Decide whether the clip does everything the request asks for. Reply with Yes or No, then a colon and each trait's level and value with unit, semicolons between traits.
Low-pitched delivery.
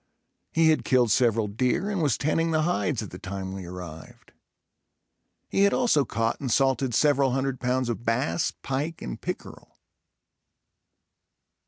Yes: low, 130 Hz